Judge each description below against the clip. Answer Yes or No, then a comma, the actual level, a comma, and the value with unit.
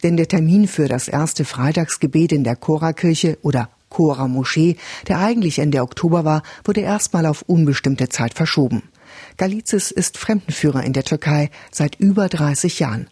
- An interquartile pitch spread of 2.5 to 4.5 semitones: Yes, average, 3.9 semitones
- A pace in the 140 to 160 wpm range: Yes, average, 150 wpm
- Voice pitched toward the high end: No, medium, 160 Hz